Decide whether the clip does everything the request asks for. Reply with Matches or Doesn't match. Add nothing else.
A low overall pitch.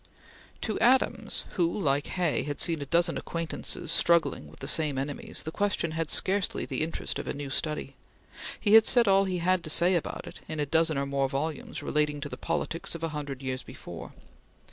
Doesn't match